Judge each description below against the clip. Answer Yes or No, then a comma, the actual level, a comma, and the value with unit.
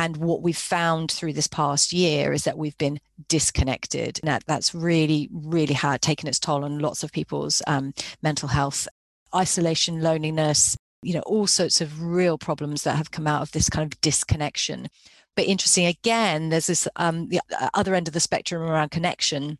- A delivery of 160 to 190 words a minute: Yes, average, 185 wpm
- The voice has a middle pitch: Yes, medium, 155 Hz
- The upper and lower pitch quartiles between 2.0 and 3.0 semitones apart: Yes, narrow, 2.4 semitones